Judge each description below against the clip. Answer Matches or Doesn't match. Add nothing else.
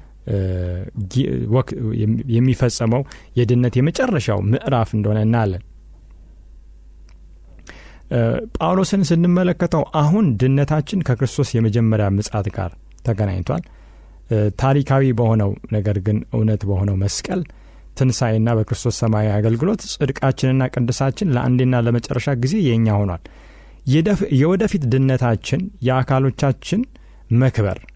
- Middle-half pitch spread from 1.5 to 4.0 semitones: Doesn't match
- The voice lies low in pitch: Matches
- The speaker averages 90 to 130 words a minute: Doesn't match